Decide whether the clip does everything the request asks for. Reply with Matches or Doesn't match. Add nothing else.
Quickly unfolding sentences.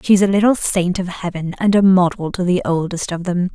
Matches